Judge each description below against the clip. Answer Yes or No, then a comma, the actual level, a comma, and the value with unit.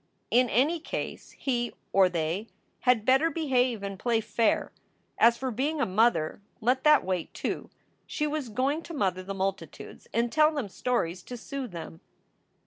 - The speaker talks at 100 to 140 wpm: No, average, 165 wpm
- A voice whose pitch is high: Yes, high, 240 Hz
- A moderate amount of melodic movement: No, wide, 5.7 semitones